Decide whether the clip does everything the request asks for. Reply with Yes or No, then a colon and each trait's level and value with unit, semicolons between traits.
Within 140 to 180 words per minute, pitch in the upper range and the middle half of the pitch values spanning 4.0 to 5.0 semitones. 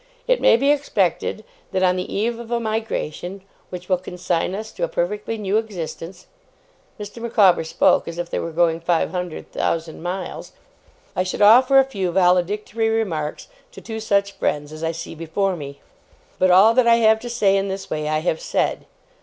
No: average, 190 wpm; high, 195 Hz; average, 4.5 semitones